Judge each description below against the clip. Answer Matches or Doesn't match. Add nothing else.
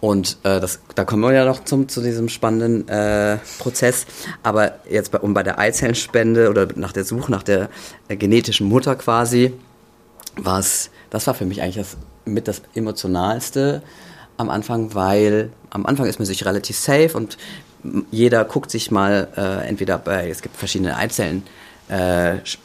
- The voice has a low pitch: Matches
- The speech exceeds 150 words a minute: Matches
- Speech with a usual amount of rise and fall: Matches